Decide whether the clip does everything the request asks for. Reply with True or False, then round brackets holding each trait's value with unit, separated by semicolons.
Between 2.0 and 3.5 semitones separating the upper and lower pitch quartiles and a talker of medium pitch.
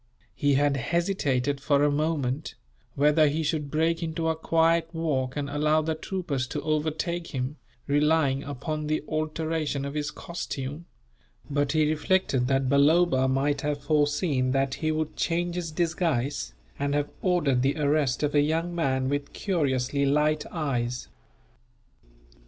True (2.6 semitones; 150 Hz)